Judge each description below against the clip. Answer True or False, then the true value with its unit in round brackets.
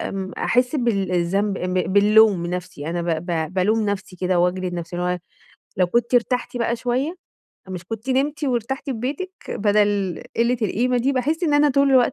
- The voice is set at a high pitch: True (215 Hz)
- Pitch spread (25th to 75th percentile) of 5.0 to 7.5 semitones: True (5.5 semitones)